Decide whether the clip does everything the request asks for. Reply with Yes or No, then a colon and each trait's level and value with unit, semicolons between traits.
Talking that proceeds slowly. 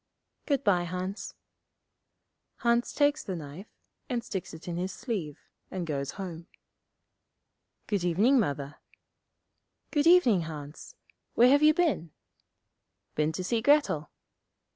Yes: slow, 120 wpm